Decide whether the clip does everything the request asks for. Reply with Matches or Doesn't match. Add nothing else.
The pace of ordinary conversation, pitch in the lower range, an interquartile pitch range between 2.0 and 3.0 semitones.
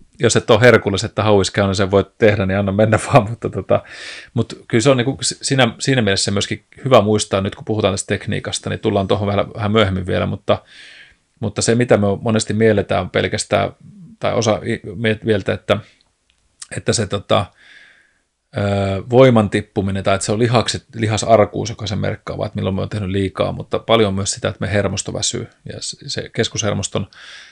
Doesn't match